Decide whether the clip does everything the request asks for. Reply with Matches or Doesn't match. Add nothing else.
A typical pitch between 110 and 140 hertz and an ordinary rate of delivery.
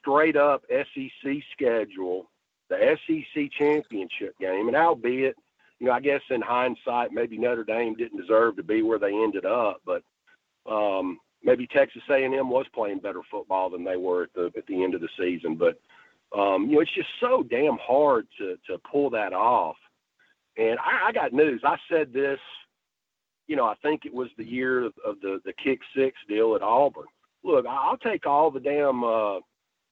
Matches